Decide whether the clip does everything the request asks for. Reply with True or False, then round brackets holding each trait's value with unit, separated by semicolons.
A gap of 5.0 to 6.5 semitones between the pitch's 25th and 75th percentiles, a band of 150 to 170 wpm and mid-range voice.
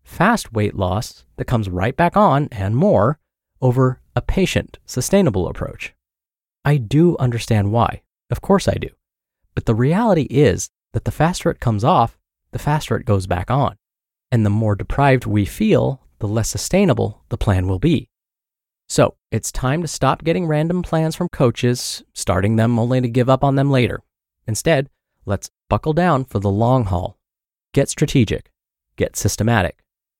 False (5.3 semitones; 165 wpm; 120 Hz)